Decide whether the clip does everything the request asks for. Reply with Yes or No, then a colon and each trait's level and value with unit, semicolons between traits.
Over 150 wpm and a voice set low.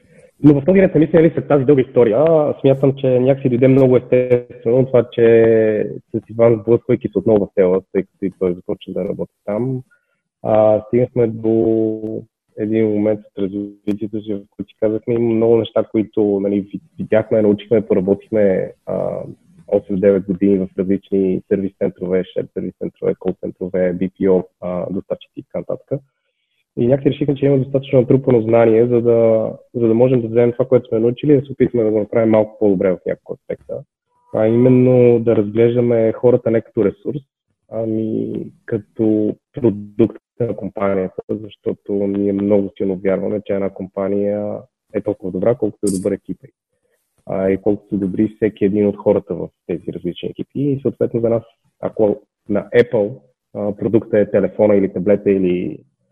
Yes: fast, 165 wpm; low, 110 Hz